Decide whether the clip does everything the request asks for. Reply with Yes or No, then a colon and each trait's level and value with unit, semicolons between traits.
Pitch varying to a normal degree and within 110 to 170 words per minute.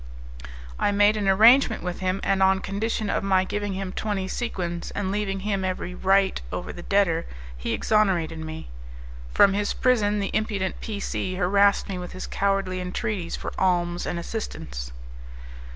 No: narrow, 2.2 semitones; average, 165 wpm